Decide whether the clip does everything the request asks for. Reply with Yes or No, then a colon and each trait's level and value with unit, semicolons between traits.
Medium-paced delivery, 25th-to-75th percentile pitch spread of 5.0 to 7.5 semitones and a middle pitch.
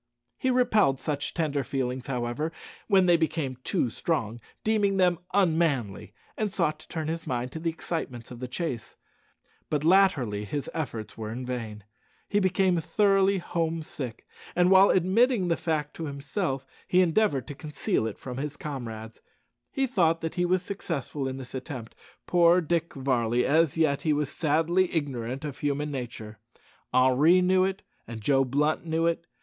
Yes: average, 165 wpm; wide, 5.4 semitones; medium, 155 Hz